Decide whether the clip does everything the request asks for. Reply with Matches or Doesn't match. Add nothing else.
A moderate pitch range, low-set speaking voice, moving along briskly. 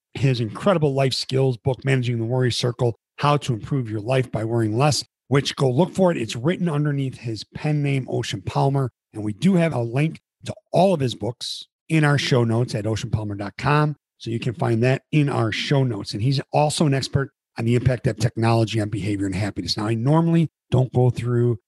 Matches